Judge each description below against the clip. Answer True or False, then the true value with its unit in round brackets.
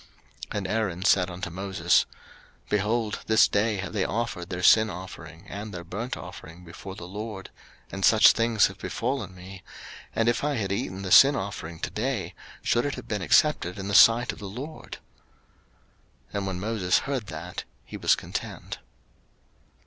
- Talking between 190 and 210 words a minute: False (175 wpm)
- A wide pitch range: False (3.7 semitones)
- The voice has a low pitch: True (100 Hz)